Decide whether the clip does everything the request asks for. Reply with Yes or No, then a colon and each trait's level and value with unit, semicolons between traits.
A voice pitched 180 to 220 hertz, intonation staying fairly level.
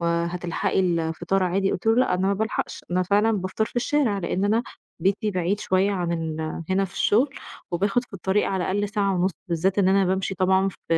Yes: high, 190 Hz; narrow, 2.3 semitones